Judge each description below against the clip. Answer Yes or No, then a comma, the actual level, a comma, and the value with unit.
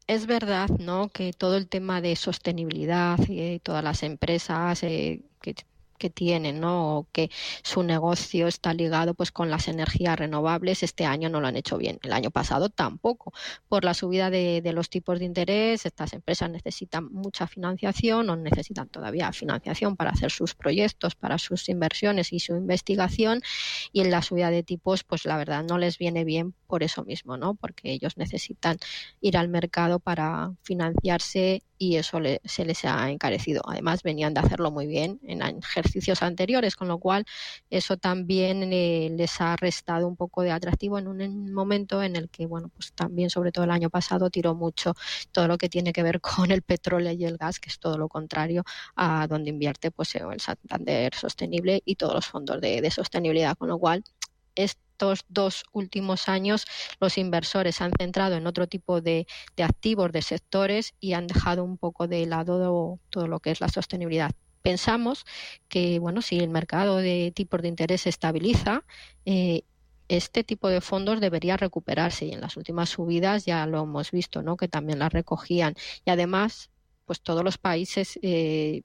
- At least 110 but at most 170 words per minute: No, average, 185 wpm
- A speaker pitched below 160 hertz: No, medium, 175 Hz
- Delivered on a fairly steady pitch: Yes, narrow, 2.2 semitones